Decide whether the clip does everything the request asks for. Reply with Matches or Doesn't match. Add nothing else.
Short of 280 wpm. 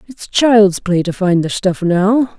Matches